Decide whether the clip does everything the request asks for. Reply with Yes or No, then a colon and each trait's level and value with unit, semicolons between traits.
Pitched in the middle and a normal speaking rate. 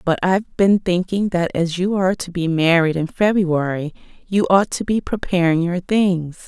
Yes: medium, 180 Hz; average, 185 wpm